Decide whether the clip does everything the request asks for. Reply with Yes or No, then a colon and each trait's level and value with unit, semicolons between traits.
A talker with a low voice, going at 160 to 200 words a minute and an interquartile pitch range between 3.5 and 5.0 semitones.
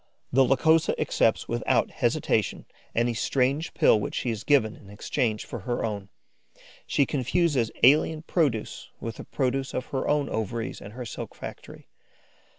No: low, 125 Hz; average, 150 wpm; average, 4.2 semitones